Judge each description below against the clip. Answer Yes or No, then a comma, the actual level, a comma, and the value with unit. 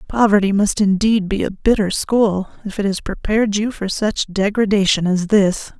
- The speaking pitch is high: Yes, high, 205 Hz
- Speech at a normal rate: Yes, average, 175 wpm